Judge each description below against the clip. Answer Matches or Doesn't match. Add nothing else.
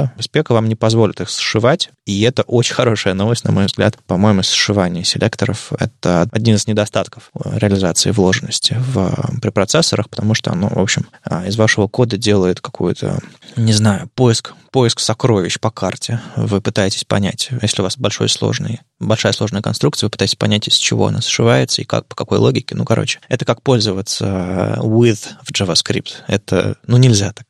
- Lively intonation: Doesn't match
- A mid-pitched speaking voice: Doesn't match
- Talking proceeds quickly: Matches